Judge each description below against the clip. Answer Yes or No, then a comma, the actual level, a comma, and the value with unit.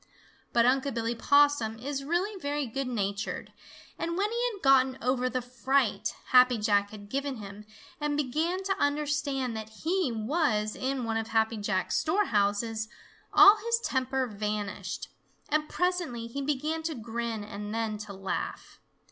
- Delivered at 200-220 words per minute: No, average, 155 wpm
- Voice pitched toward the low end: No, very high, 255 Hz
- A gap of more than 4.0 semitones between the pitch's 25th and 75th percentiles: Yes, average, 5.1 semitones